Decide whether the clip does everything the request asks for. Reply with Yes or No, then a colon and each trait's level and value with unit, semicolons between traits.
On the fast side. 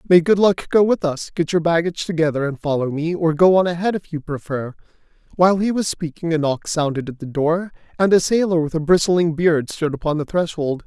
Yes: fast, 225 wpm